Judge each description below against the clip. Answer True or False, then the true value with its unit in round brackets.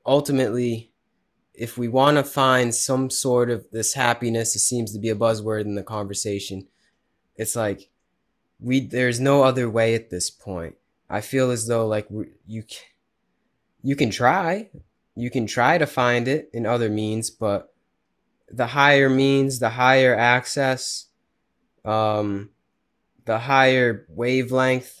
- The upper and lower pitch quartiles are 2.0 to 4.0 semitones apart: True (2.9 semitones)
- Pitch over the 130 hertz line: False (120 Hz)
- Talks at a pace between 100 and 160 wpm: True (145 wpm)